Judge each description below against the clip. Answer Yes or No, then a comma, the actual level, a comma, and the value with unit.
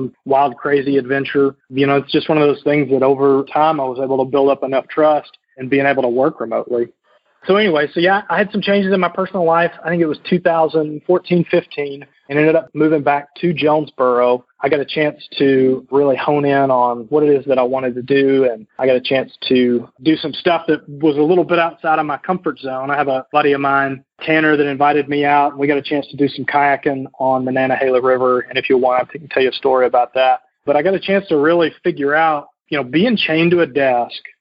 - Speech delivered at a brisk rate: Yes, fast, 245 wpm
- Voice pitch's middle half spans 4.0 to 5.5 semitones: No, average, 2.9 semitones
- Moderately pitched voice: Yes, medium, 145 Hz